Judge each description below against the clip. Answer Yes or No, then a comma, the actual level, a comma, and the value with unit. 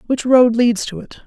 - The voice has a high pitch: Yes, high, 235 Hz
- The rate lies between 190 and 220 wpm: No, fast, 235 wpm